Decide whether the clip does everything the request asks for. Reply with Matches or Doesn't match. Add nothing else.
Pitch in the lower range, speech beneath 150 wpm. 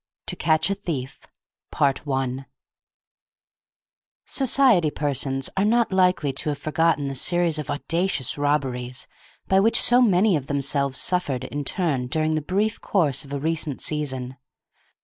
Doesn't match